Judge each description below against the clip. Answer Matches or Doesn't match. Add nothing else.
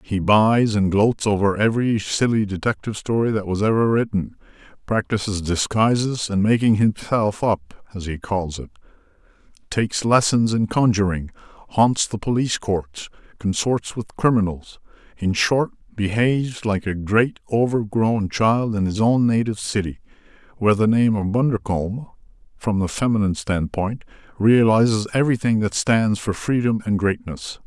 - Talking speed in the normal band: Doesn't match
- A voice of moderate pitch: Doesn't match